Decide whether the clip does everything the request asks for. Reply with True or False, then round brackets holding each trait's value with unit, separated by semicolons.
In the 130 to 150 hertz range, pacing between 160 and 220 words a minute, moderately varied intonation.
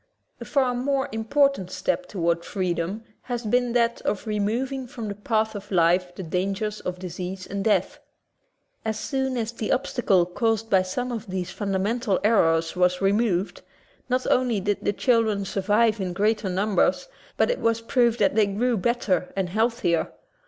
False (210 Hz; 175 wpm; 4.1 semitones)